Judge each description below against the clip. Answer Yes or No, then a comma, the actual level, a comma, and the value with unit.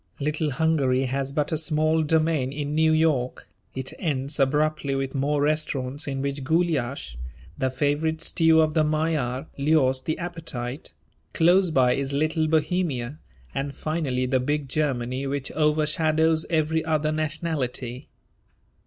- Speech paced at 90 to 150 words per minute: Yes, slow, 135 wpm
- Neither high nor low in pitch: Yes, medium, 150 Hz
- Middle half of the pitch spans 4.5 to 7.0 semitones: No, average, 2.9 semitones